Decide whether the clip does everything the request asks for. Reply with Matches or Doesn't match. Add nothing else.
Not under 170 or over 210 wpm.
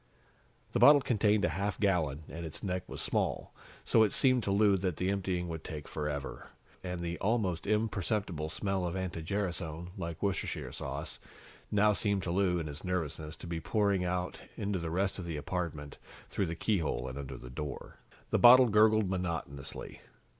Matches